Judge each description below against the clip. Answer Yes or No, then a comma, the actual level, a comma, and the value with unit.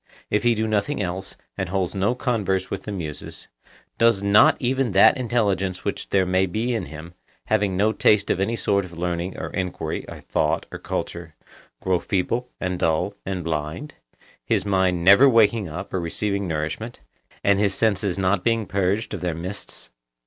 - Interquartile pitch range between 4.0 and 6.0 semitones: No, average, 3.2 semitones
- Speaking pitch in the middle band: No, very low, 95 Hz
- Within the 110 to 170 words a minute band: No, average, 180 wpm